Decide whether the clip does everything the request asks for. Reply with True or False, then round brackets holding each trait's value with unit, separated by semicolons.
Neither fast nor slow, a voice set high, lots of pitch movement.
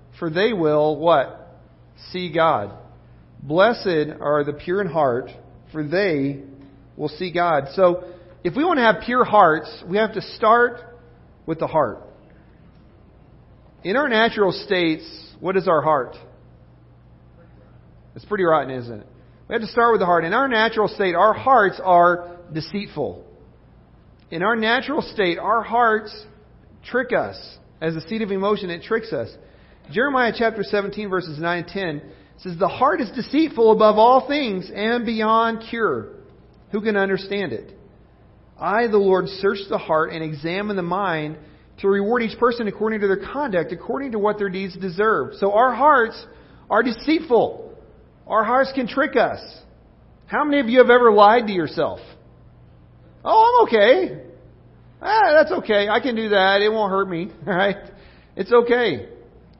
True (160 wpm; 200 Hz; 5.7 semitones)